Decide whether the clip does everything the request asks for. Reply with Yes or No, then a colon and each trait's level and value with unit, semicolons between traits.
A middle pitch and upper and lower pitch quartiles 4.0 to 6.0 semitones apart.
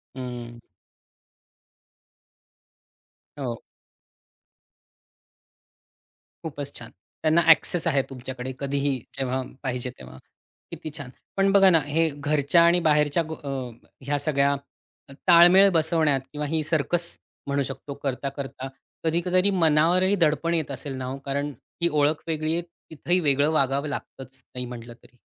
No: medium, 145 Hz; average, 3.3 semitones